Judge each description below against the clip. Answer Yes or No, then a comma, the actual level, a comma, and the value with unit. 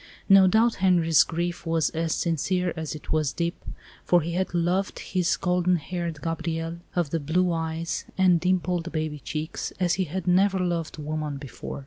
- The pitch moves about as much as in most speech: No, narrow, 2.1 semitones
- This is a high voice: No, medium, 170 Hz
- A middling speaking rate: Yes, average, 170 wpm